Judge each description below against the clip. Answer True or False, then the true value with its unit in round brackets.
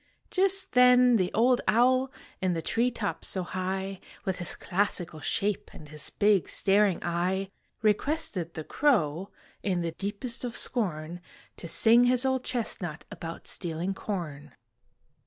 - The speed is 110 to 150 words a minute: True (140 wpm)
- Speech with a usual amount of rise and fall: False (5.8 semitones)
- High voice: True (195 Hz)